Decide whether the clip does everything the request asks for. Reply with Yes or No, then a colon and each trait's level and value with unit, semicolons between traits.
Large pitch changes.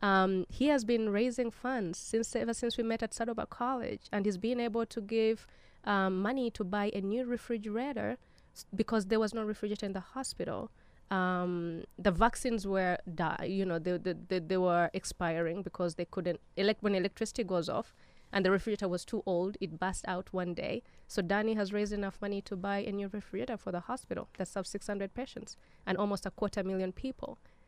No: average, 3.4 semitones